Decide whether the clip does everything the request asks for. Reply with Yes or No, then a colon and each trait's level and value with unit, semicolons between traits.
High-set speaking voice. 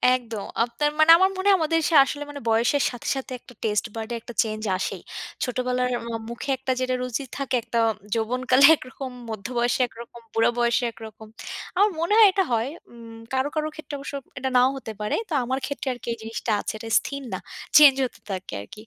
Yes: very high, 250 Hz